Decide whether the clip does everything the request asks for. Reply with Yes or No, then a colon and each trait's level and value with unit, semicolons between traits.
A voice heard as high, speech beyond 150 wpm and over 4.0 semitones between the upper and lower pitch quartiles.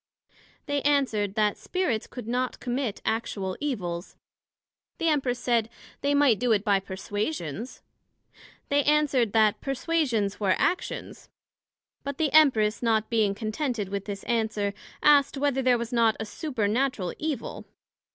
No: high, 235 Hz; slow, 135 wpm; average, 5.1 semitones